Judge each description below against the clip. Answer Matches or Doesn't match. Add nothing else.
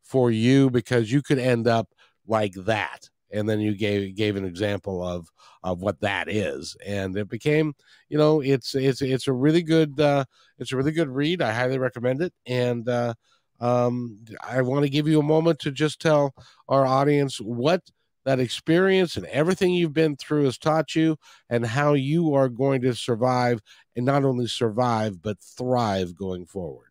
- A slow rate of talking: Doesn't match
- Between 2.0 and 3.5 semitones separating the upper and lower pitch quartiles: Doesn't match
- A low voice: Matches